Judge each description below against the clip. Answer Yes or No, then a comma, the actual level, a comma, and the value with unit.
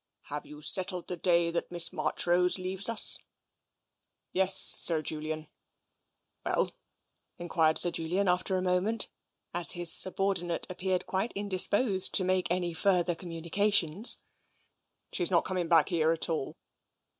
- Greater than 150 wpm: No, average, 145 wpm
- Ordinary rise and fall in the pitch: No, narrow, 2.0 semitones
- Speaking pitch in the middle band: Yes, medium, 180 Hz